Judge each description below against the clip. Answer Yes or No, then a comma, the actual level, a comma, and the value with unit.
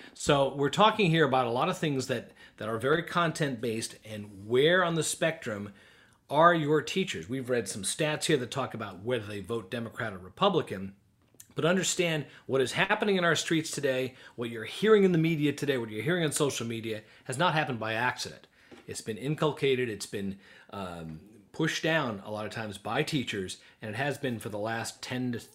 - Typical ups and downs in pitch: No, wide, 6.0 semitones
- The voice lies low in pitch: Yes, low, 130 Hz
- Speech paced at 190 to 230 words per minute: Yes, average, 200 wpm